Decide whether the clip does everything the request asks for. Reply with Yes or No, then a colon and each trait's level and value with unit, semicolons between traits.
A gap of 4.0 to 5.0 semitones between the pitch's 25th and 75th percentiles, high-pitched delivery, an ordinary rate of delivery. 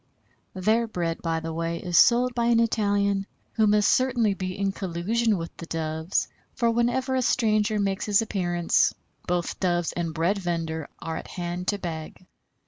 Yes: average, 4.5 semitones; high, 195 Hz; average, 170 wpm